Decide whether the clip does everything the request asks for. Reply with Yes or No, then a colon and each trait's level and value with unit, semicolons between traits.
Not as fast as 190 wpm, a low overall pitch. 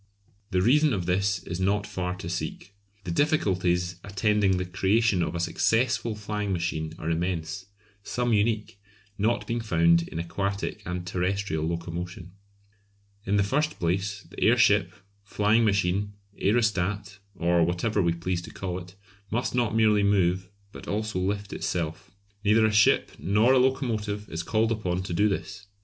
Yes: average, 155 wpm; low, 100 Hz